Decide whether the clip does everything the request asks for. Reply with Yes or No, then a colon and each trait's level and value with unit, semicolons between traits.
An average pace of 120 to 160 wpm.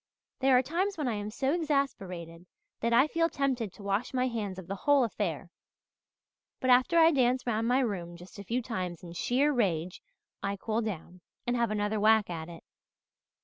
No: average, 190 wpm